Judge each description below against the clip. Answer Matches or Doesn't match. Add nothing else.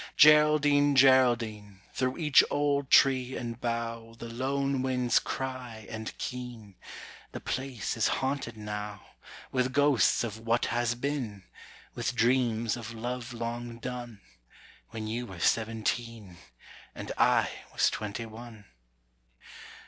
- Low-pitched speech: Matches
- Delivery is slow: Matches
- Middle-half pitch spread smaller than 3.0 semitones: Matches